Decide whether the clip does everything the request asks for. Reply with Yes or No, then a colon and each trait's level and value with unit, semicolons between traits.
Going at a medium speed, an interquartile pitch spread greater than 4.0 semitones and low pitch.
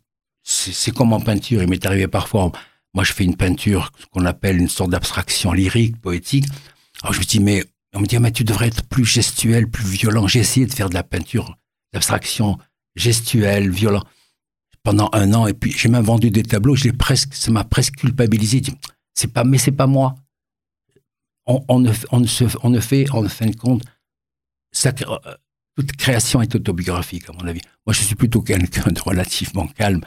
Yes: average, 210 wpm; average, 4.4 semitones; low, 110 Hz